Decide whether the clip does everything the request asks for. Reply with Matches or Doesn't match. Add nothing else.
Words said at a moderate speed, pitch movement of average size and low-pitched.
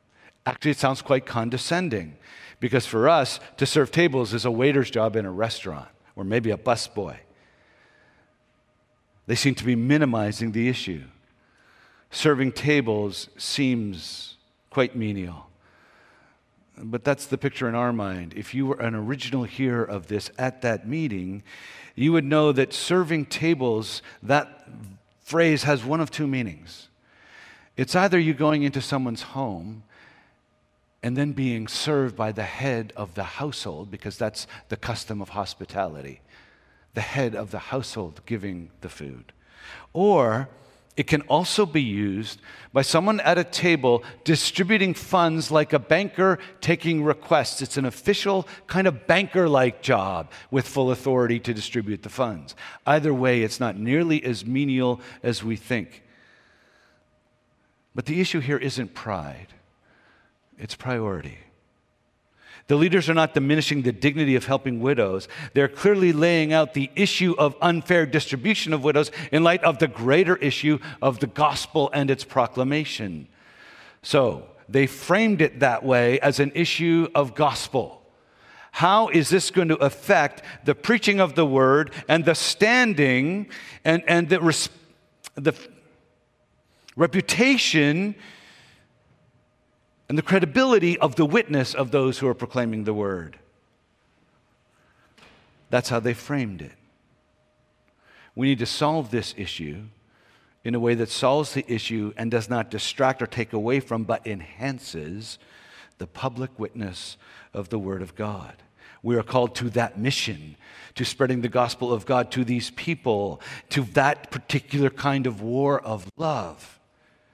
Matches